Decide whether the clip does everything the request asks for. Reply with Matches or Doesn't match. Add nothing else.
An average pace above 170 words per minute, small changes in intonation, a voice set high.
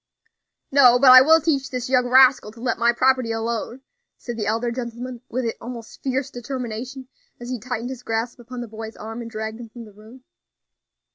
Matches